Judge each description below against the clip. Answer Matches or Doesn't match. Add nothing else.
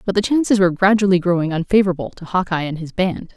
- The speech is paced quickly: Matches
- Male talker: Doesn't match